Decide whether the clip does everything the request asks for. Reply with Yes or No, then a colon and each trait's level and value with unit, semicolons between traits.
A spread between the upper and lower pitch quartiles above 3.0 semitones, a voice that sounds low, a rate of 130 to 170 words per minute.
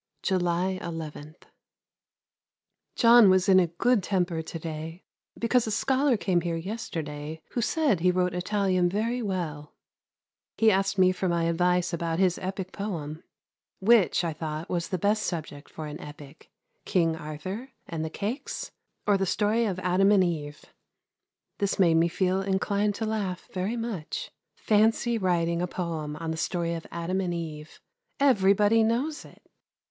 No: average, 3.8 semitones; medium, 185 Hz; average, 155 wpm